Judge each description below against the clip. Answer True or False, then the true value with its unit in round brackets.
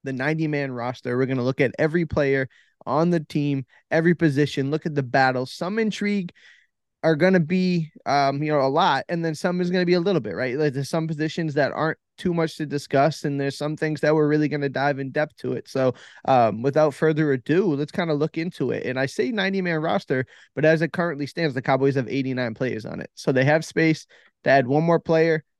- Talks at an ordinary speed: False (235 wpm)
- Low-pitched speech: False (150 Hz)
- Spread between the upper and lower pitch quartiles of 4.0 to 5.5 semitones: False (3.0 semitones)